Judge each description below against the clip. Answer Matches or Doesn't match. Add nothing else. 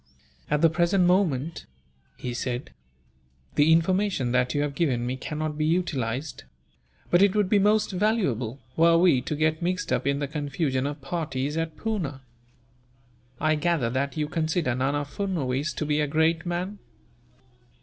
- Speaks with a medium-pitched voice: Matches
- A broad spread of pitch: Doesn't match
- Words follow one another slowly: Doesn't match